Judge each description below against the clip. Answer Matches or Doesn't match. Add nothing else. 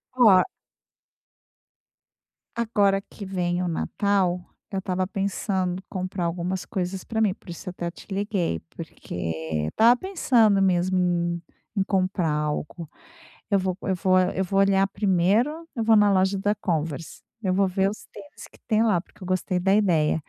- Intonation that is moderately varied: Doesn't match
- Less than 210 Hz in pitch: Matches